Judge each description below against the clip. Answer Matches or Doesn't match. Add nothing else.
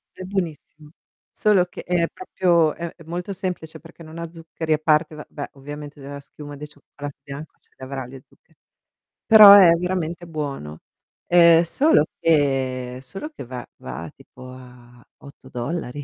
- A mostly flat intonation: Doesn't match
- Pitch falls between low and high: Matches